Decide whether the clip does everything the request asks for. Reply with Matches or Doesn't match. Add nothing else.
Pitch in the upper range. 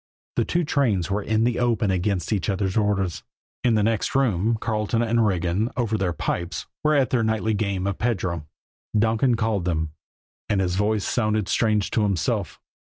Doesn't match